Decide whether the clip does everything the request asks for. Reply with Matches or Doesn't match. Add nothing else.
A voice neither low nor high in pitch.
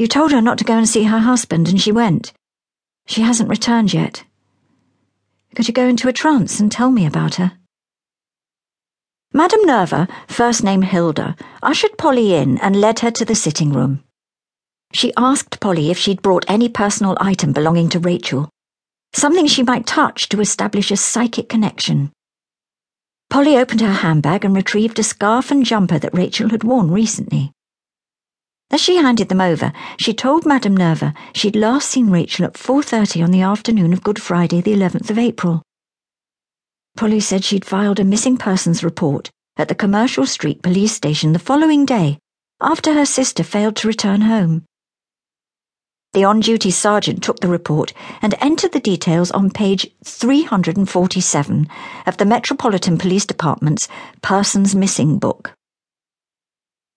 Doesn't match